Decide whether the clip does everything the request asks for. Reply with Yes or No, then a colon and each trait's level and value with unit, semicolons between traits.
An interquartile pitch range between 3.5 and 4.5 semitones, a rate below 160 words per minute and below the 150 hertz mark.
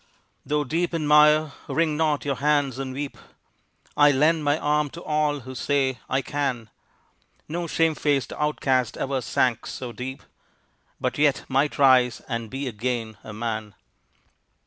No: average, 2.9 semitones; average, 150 wpm; medium, 140 Hz